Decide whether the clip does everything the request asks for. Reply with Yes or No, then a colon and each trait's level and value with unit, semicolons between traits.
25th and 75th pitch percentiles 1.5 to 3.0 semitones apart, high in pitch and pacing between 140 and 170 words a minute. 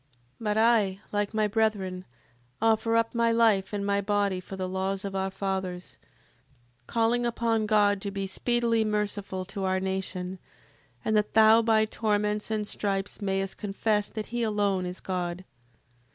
Yes: narrow, 2.4 semitones; high, 205 Hz; average, 160 wpm